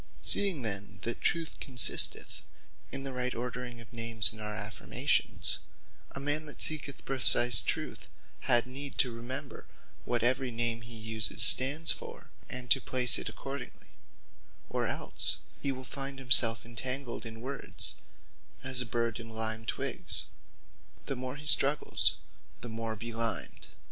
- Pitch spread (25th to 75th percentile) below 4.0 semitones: Yes, average, 2.9 semitones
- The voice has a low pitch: Yes, low, 125 Hz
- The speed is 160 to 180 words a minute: No, average, 145 wpm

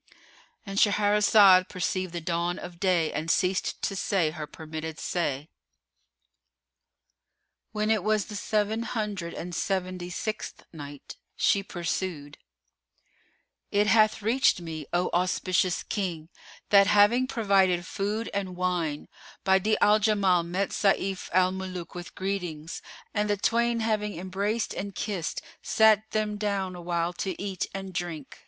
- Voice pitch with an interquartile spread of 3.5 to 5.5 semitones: No, average, 3.0 semitones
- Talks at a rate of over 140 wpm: No, slow, 135 wpm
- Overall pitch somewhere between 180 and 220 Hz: Yes, high, 190 Hz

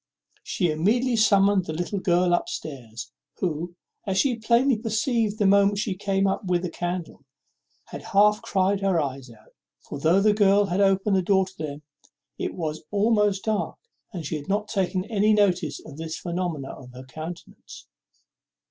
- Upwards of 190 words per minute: No, average, 175 wpm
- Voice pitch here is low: No, high, 190 Hz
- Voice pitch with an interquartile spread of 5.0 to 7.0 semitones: No, average, 3.8 semitones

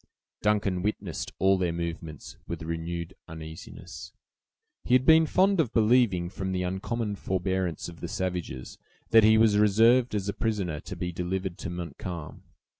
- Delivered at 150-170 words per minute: Yes, average, 155 wpm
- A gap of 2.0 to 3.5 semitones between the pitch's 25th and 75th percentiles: No, average, 3.9 semitones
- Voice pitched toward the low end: Yes, very low, 95 Hz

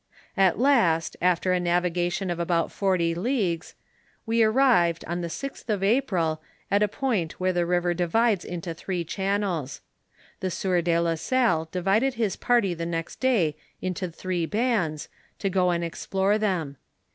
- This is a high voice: No, medium, 180 Hz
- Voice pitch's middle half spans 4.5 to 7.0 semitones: No, average, 3.6 semitones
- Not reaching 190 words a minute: Yes, average, 160 wpm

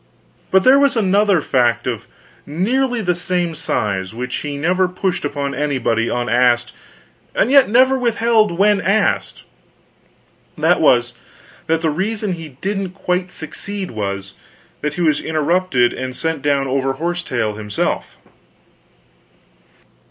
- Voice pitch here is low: No, medium, 165 Hz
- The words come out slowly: Yes, slow, 130 wpm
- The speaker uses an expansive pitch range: Yes, wide, 7.2 semitones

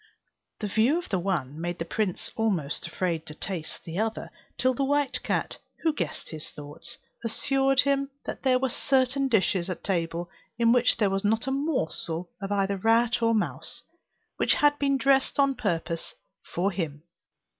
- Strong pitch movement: Yes, wide, 7.4 semitones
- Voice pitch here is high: Yes, high, 220 Hz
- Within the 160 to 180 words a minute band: Yes, average, 175 wpm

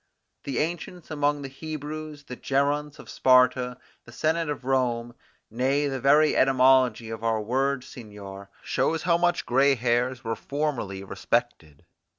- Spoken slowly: No, average, 145 wpm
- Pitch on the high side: No, low, 130 Hz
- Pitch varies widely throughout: No, average, 3.5 semitones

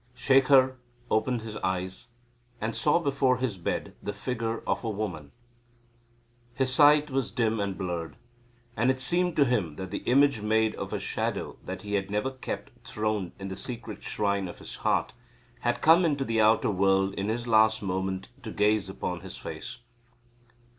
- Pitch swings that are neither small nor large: Yes, average, 4.9 semitones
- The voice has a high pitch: No, low, 110 Hz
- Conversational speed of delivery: Yes, average, 175 wpm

